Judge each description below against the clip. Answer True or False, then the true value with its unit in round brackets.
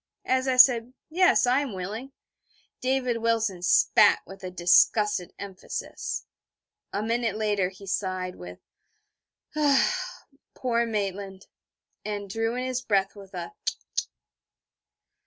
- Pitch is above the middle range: True (215 Hz)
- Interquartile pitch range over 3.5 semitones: True (4.5 semitones)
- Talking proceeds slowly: True (120 wpm)